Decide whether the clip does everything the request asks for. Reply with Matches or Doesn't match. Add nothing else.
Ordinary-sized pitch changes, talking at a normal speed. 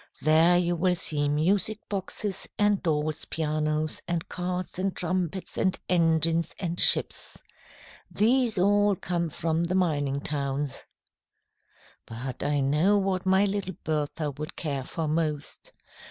Doesn't match